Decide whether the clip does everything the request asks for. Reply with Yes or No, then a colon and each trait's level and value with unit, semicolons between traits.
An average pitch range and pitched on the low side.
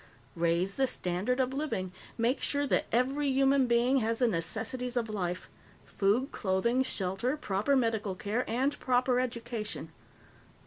No: average, 4.4 semitones; high, 240 Hz